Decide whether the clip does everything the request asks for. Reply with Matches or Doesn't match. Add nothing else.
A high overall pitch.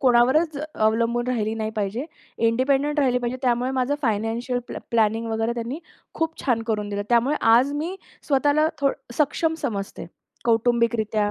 Matches